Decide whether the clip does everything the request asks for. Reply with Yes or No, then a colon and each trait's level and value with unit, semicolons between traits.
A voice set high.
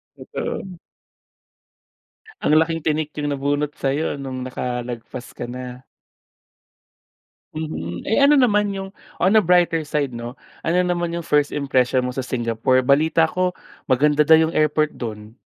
No: medium, 145 Hz